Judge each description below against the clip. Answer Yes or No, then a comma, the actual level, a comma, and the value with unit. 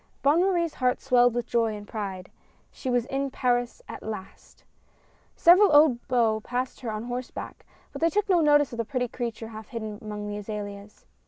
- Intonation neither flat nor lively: Yes, average, 4.3 semitones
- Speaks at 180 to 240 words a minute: Yes, average, 185 wpm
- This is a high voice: Yes, high, 245 Hz